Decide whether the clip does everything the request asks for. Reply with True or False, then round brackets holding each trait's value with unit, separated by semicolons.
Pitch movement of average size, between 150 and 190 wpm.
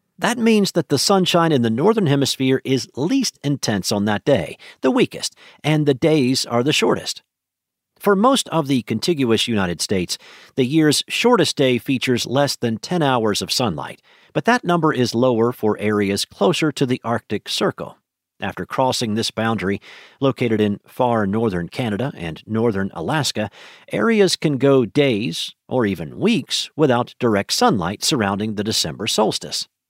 False (6.0 semitones; 160 wpm)